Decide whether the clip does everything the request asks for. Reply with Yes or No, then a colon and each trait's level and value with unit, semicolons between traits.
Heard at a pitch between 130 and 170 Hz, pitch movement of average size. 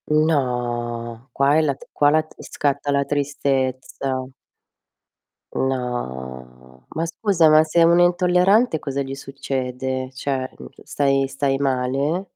Yes: low, 135 Hz; average, 3.2 semitones